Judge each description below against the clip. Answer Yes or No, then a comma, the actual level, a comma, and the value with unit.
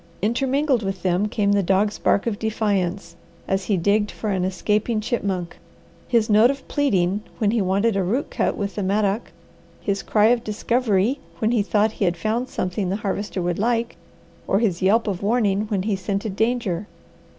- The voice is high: Yes, high, 205 Hz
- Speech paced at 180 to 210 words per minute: Yes, average, 185 wpm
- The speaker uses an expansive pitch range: No, average, 2.7 semitones